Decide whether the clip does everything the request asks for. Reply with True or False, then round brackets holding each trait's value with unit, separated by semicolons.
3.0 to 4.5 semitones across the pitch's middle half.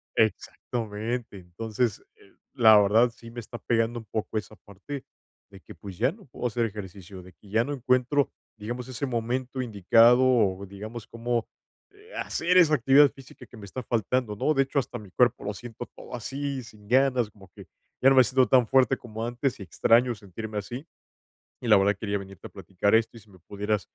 True (3.7 semitones)